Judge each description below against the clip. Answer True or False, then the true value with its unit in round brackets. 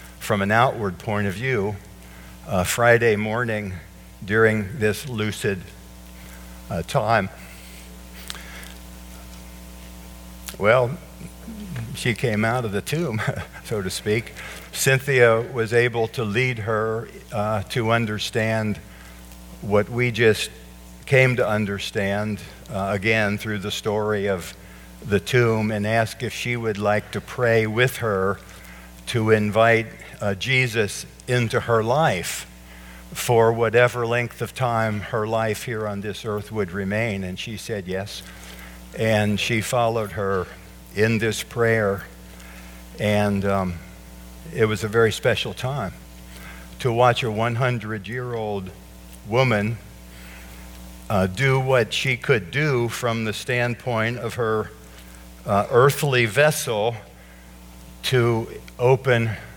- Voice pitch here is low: True (105 Hz)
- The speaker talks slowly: True (120 wpm)